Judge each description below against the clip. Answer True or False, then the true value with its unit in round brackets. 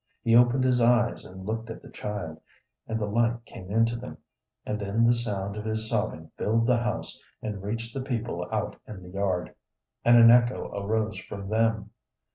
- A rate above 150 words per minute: True (190 wpm)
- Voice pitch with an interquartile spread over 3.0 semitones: False (2.7 semitones)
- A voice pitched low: True (110 Hz)